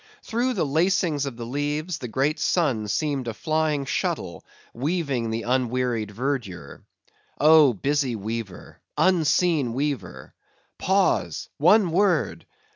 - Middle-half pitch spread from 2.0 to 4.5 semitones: No, average, 5.3 semitones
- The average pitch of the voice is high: No, medium, 140 Hz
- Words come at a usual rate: No, slow, 110 wpm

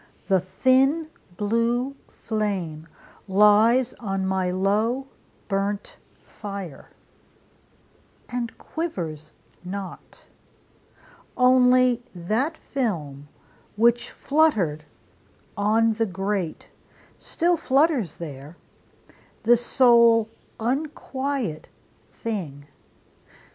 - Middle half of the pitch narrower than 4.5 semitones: No, average, 5.1 semitones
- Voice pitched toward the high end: Yes, high, 220 Hz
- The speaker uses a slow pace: Yes, slow, 70 wpm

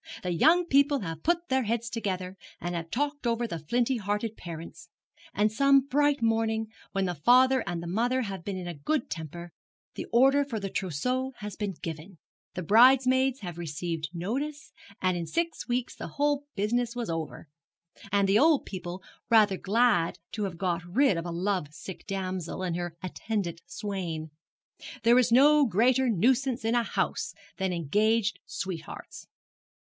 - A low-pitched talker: No, high, 210 Hz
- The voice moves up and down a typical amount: No, wide, 6.3 semitones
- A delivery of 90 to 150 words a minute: No, average, 165 wpm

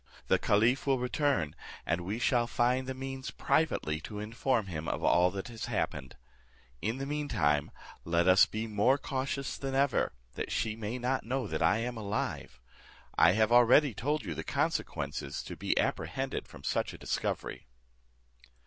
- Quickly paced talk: No, average, 165 wpm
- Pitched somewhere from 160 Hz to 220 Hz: No, low, 115 Hz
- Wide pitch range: Yes, wide, 5.8 semitones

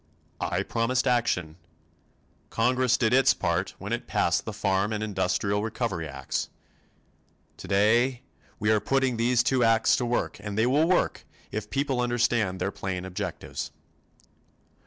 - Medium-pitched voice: No, low, 115 Hz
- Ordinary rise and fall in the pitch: Yes, average, 3.7 semitones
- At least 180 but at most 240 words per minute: No, average, 145 wpm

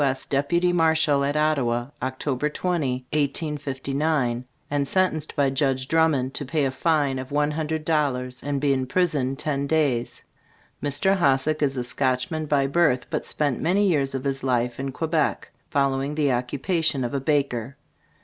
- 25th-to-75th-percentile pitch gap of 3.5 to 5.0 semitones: No, average, 2.7 semitones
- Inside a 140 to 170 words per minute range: Yes, average, 160 wpm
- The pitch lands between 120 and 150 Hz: Yes, medium, 140 Hz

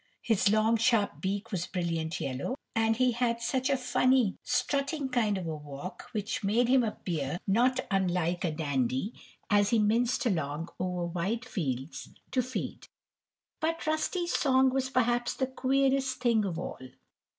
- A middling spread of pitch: No, wide, 6.3 semitones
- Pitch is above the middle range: Yes, high, 225 Hz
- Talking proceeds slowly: No, average, 155 wpm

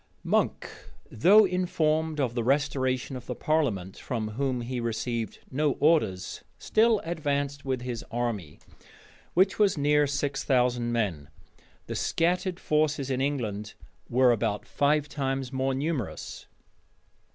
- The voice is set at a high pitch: No, low, 135 Hz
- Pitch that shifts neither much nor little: Yes, average, 4.3 semitones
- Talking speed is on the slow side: Yes, slow, 130 wpm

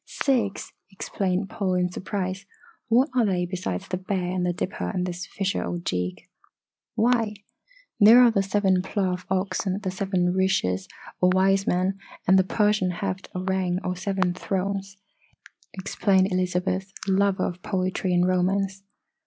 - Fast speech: No, average, 145 wpm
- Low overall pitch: No, high, 190 Hz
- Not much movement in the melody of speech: Yes, narrow, 1.4 semitones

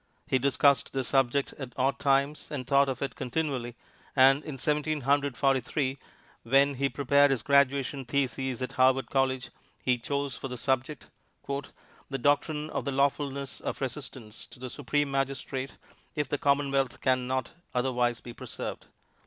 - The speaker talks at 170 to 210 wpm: No, average, 160 wpm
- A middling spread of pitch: No, narrow, 1.5 semitones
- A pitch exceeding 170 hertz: No, low, 135 Hz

